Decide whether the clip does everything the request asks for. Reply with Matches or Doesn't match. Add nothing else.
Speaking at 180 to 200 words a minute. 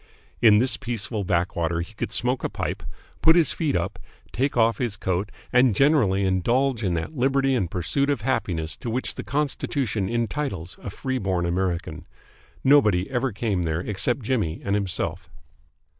Doesn't match